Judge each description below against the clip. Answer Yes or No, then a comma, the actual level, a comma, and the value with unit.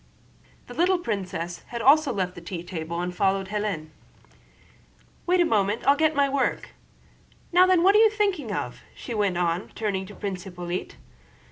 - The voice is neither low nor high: No, high, 205 Hz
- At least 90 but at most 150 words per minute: No, average, 170 wpm